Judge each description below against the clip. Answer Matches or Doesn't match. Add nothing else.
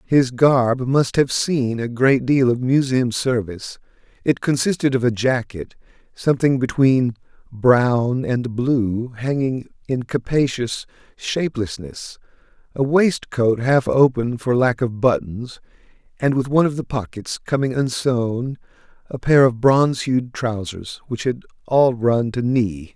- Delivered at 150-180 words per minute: Doesn't match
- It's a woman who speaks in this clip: Doesn't match